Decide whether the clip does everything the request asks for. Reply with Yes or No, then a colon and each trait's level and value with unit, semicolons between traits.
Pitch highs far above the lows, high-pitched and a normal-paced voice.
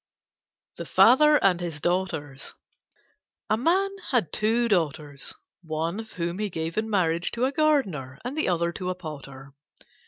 No: wide, 5.9 semitones; medium, 180 Hz; average, 155 wpm